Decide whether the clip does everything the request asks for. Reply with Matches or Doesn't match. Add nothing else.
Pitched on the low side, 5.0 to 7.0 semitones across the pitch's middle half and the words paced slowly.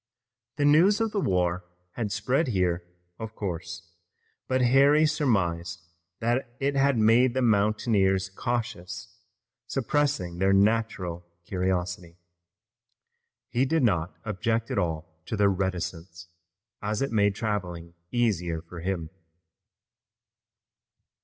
Matches